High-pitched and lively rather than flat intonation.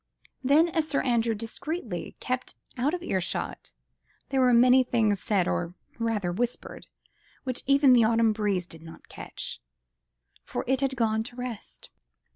No: high, 240 Hz; average, 3.6 semitones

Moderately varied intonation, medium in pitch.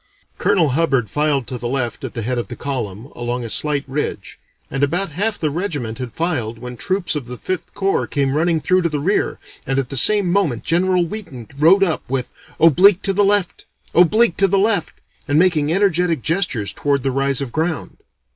No: wide, 5.8 semitones; medium, 155 Hz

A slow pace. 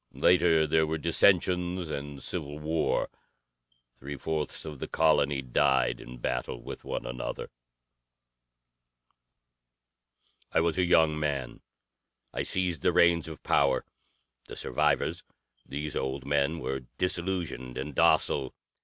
Yes: slow, 120 wpm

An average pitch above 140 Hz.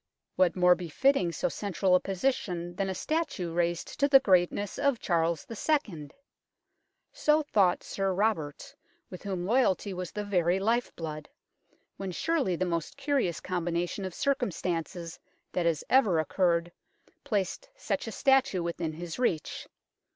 Yes: medium, 185 Hz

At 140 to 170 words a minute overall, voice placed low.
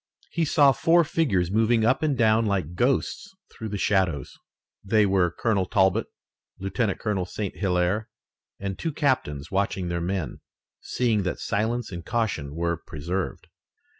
Yes: average, 145 wpm; low, 100 Hz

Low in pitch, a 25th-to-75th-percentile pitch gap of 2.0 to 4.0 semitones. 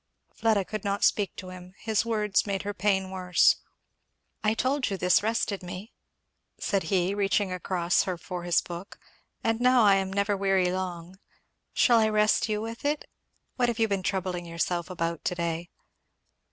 No: high, 195 Hz; average, 2.9 semitones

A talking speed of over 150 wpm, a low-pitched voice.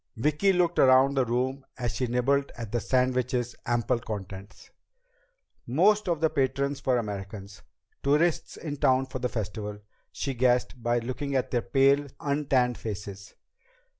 No: average, 145 wpm; low, 130 Hz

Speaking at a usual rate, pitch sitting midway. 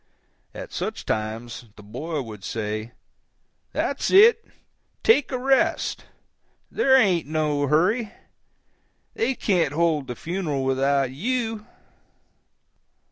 No: slow, 100 wpm; medium, 155 Hz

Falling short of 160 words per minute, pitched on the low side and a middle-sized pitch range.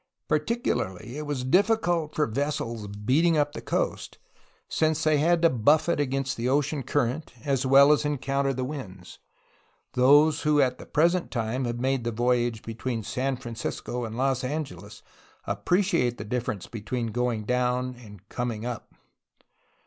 Yes: average, 150 wpm; low, 130 Hz; average, 3.9 semitones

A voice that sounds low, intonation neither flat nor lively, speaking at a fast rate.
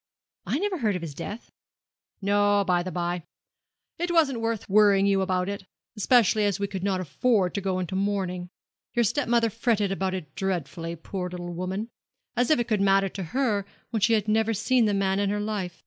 No: high, 200 Hz; average, 3.1 semitones; fast, 210 wpm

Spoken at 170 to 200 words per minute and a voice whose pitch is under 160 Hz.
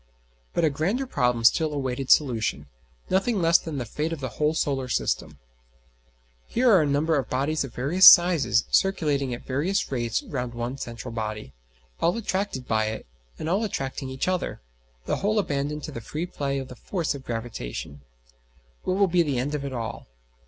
Yes: average, 185 wpm; medium, 140 Hz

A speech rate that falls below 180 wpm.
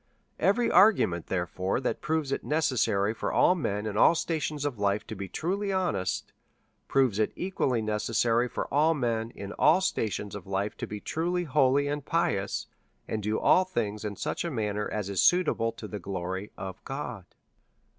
No: average, 195 wpm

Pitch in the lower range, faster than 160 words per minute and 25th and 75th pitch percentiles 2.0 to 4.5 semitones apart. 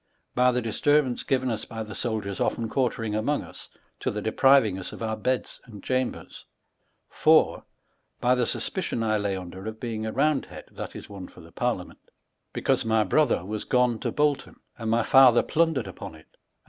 Yes: low, 115 Hz; average, 190 wpm; average, 3.1 semitones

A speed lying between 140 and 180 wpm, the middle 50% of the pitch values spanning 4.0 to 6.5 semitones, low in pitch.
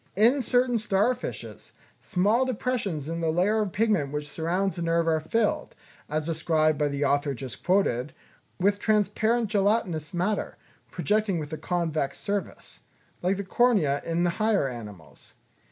No: average, 155 wpm; wide, 5.5 semitones; medium, 180 Hz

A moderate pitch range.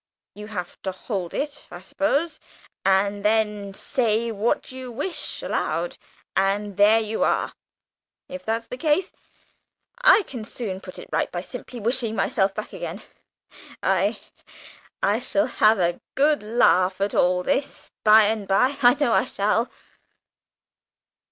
Yes: average, 4.4 semitones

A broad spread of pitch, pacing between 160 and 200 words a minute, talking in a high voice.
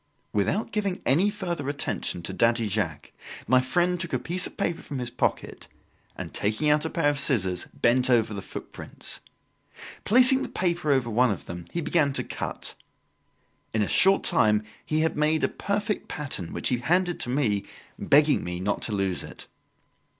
No: wide, 7.8 semitones; average, 180 wpm; medium, 140 Hz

